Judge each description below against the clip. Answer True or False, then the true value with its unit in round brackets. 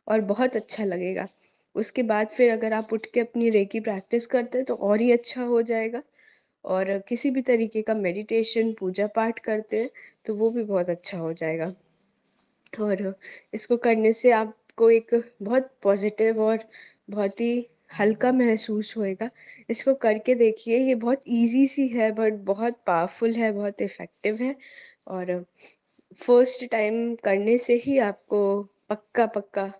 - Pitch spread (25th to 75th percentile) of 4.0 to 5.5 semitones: False (2.5 semitones)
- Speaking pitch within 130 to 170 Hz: False (225 Hz)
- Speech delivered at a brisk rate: False (155 wpm)